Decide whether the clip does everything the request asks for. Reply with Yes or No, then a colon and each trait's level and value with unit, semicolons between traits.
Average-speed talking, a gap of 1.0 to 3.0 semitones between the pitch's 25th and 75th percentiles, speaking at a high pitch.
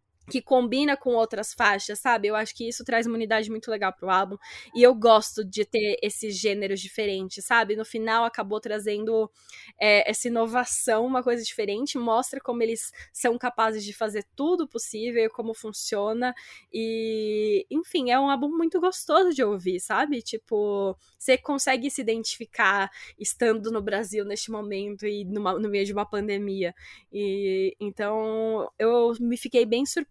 Yes: average, 165 wpm; average, 2.7 semitones; high, 225 Hz